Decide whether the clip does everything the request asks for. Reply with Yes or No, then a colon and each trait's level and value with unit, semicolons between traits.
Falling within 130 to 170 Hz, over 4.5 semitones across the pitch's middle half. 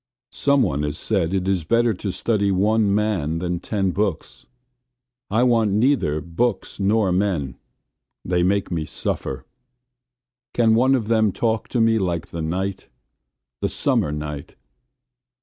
No: very low, 95 Hz; average, 5.1 semitones